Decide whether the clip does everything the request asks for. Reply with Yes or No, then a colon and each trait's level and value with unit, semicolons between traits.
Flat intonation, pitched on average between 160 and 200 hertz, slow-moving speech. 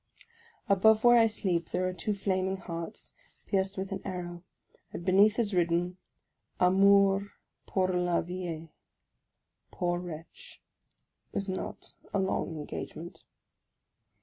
Yes: narrow, 2.1 semitones; medium, 185 Hz; slow, 125 wpm